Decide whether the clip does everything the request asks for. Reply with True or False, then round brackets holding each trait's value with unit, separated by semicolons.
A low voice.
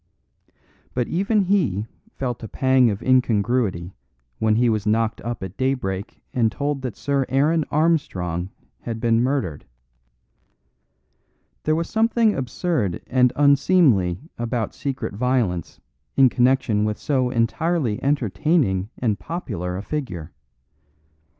True (125 Hz)